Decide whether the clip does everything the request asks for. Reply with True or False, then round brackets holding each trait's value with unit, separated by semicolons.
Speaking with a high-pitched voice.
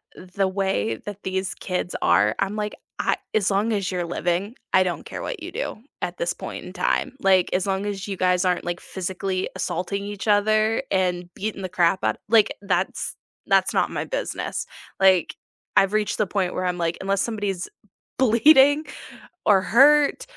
True (195 Hz)